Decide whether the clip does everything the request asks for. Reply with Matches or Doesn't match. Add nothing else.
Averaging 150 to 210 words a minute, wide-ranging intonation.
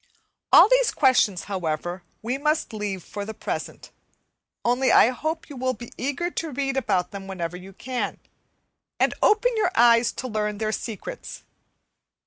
Matches